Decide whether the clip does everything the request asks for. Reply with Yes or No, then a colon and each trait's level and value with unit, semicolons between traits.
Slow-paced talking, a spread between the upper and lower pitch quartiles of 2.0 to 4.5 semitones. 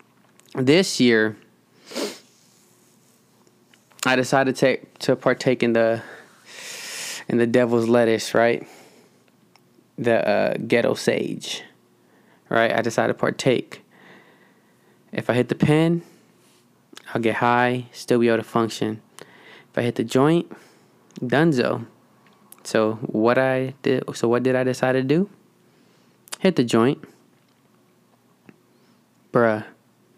Yes: slow, 115 wpm; average, 3.1 semitones